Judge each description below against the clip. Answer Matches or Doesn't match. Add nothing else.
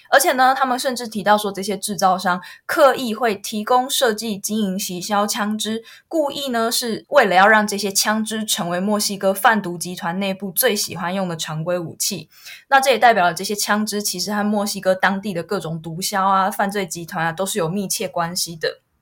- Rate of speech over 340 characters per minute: Doesn't match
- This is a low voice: Doesn't match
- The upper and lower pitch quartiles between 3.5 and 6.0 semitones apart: Doesn't match